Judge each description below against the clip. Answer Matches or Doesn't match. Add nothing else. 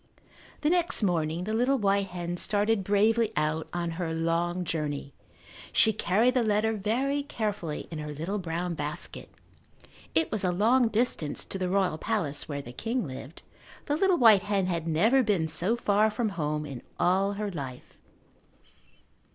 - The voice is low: Doesn't match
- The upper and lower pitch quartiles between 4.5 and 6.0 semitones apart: Matches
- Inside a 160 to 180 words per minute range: Matches